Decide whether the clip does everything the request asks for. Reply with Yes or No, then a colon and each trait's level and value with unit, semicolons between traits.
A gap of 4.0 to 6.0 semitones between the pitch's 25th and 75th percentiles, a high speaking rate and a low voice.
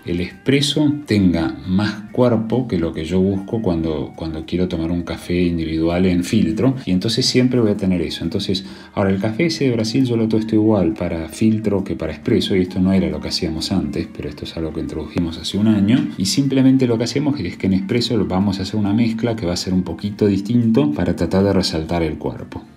Yes: average, 4.7 semitones; fast, 225 wpm; very low, 95 Hz